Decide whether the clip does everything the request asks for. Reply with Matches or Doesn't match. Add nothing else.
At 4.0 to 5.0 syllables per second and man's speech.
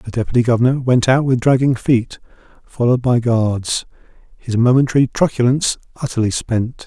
Doesn't match